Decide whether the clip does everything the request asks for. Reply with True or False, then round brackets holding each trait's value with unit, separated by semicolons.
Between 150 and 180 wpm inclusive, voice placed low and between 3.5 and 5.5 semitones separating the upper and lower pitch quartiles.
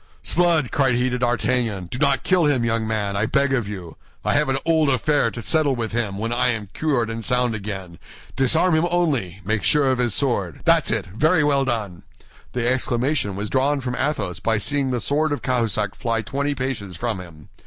False (205 wpm; 125 Hz; 4.7 semitones)